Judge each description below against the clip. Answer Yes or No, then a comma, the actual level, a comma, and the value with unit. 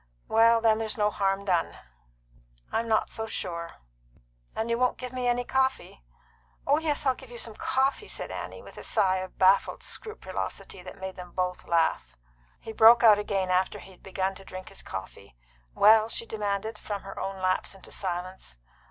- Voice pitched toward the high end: Yes, high, 205 Hz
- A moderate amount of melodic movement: Yes, average, 3.7 semitones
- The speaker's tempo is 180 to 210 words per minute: Yes, average, 185 wpm